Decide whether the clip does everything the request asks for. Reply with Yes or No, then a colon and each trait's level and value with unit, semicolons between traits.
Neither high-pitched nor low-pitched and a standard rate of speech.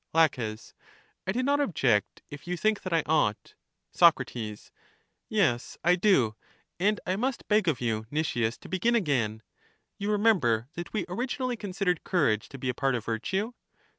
Yes: medium, 175 Hz; average, 165 wpm